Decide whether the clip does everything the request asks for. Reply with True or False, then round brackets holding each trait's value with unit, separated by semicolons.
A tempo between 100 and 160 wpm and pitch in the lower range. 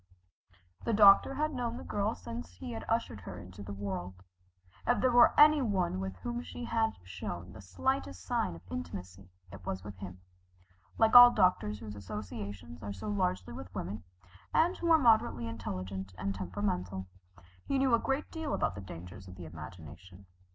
False (175 wpm; 100 Hz)